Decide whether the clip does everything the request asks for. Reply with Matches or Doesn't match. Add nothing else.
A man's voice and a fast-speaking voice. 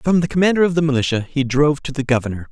Matches